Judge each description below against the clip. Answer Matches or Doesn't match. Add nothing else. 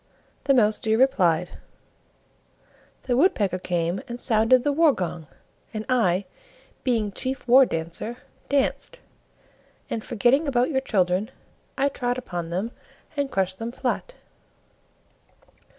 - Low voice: Doesn't match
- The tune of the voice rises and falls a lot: Matches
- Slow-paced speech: Matches